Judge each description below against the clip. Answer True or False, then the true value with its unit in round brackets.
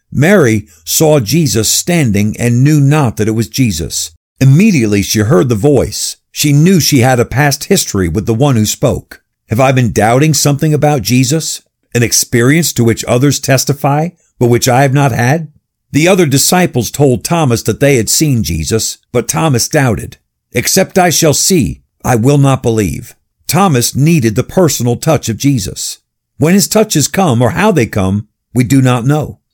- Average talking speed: True (175 wpm)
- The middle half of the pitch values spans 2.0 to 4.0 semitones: False (5.1 semitones)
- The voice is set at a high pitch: False (130 Hz)